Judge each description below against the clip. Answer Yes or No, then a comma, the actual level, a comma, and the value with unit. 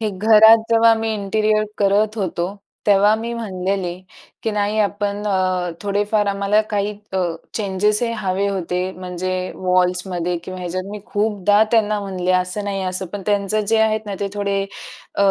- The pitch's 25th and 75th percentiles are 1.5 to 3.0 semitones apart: Yes, narrow, 2.4 semitones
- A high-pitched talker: Yes, high, 200 Hz